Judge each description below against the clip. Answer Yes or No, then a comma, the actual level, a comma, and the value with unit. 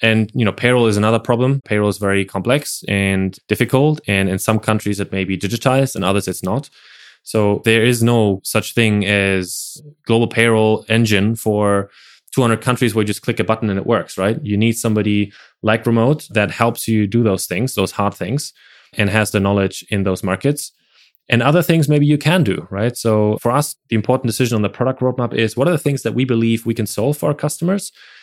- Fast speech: Yes, fast, 215 wpm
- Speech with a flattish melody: No, average, 3.8 semitones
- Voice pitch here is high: No, low, 115 Hz